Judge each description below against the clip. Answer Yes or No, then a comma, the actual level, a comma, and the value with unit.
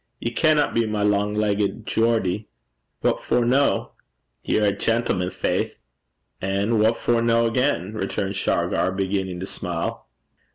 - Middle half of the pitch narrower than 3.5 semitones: Yes, average, 3.1 semitones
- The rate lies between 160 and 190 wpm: No, slow, 135 wpm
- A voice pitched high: No, low, 105 Hz